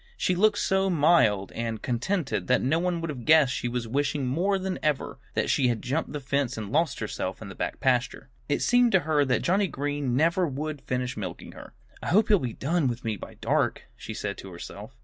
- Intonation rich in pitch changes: Yes, wide, 5.7 semitones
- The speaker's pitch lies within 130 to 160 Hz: Yes, medium, 140 Hz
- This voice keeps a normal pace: No, fast, 225 wpm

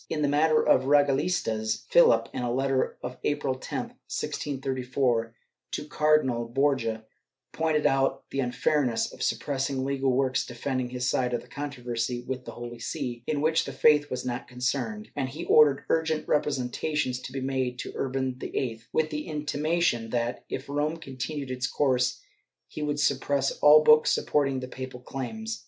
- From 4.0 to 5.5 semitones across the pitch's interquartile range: No, average, 2.9 semitones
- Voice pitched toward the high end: No, low, 135 Hz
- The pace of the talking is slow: No, average, 165 wpm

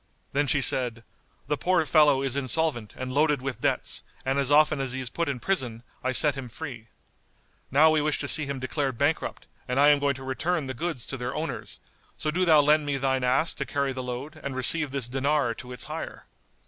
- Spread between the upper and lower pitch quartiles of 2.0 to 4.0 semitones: Yes, average, 2.8 semitones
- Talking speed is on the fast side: Yes, fast, 225 wpm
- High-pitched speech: No, medium, 140 Hz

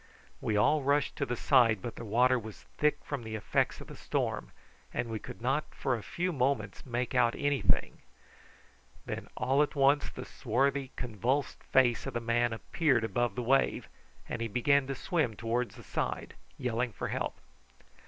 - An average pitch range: Yes, average, 3.2 semitones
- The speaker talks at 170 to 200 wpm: Yes, average, 180 wpm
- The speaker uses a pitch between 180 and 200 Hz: No, low, 125 Hz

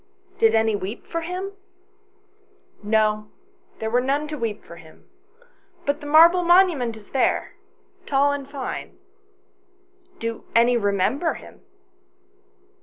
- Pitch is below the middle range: No, very high, 255 Hz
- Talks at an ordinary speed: No, slow, 125 wpm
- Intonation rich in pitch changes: Yes, wide, 6.2 semitones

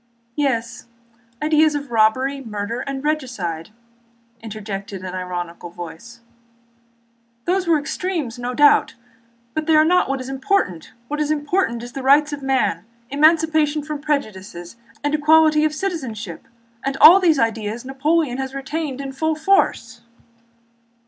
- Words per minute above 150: No, average, 140 wpm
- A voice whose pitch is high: Yes, very high, 275 Hz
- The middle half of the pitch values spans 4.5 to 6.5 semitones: Yes, average, 5.3 semitones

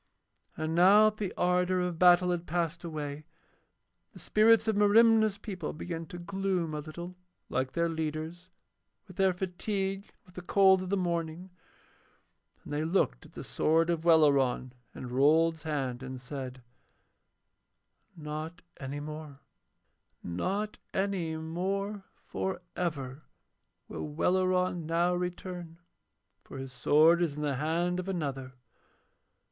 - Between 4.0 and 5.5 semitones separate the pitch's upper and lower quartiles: No, average, 3.5 semitones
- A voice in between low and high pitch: Yes, medium, 170 Hz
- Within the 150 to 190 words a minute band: No, slow, 135 wpm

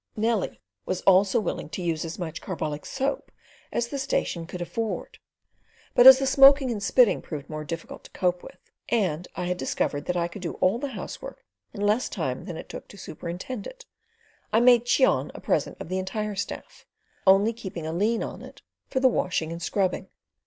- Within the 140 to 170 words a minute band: No, average, 195 wpm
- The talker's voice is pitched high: Yes, high, 195 Hz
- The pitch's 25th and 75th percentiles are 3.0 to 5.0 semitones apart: No, wide, 5.5 semitones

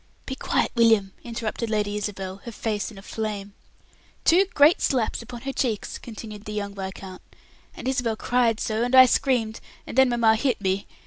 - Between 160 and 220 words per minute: Yes, average, 180 wpm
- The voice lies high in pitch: Yes, high, 220 Hz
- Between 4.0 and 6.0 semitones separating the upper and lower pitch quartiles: No, average, 3.0 semitones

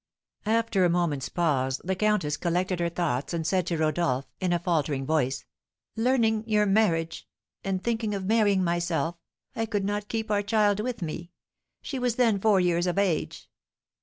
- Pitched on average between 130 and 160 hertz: No, medium, 185 Hz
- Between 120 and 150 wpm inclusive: No, average, 170 wpm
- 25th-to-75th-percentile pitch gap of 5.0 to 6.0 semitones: No, average, 4.2 semitones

